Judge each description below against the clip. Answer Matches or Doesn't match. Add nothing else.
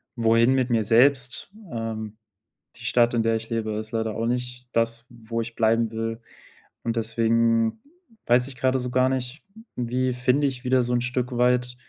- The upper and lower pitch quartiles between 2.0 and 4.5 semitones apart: Doesn't match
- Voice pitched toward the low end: Matches